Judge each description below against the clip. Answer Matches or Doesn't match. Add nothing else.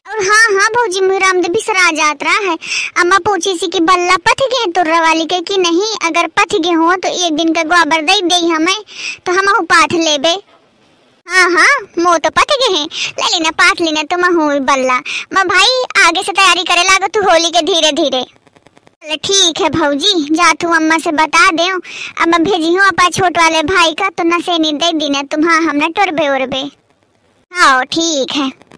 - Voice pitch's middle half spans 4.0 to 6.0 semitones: Doesn't match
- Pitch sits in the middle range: Doesn't match